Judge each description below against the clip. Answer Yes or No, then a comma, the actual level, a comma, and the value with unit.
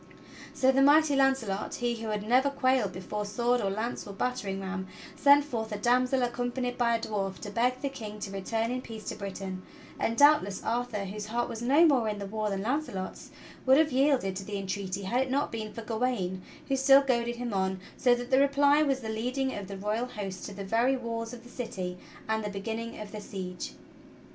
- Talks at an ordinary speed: No, fast, 220 wpm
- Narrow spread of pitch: No, average, 4.1 semitones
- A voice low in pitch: No, high, 230 Hz